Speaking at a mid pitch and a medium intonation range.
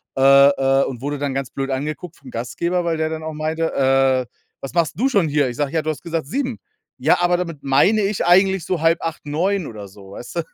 Yes: medium, 155 Hz; average, 4.1 semitones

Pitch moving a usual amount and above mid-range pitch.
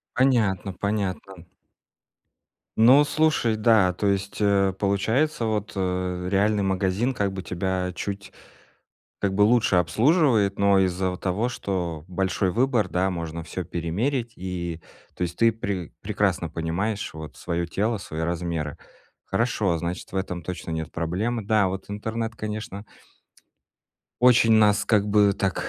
No: average, 3.3 semitones; low, 100 Hz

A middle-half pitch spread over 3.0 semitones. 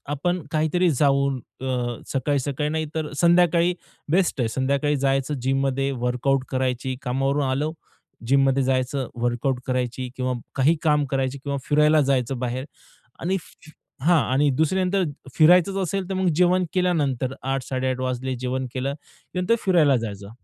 Yes: average, 3.5 semitones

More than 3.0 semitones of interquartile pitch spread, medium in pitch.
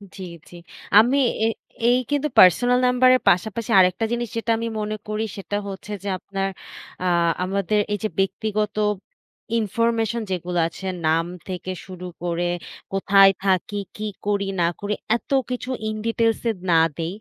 No: average, 3.6 semitones; high, 205 Hz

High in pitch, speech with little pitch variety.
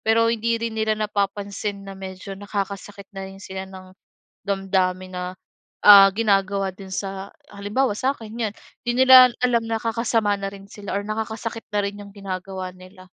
Yes: high, 200 Hz; narrow, 2.3 semitones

